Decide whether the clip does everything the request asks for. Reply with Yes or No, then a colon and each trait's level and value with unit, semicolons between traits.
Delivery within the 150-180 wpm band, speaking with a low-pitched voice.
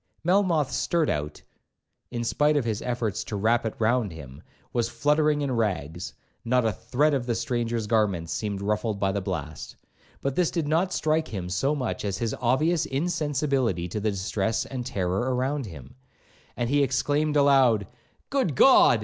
Yes: average, 165 wpm; low, 120 Hz